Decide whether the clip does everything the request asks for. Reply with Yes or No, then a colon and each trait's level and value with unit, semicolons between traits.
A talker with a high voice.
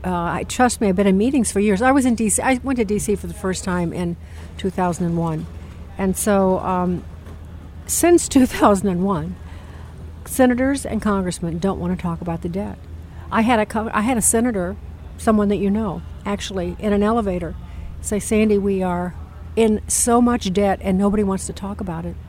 Yes: high, 195 Hz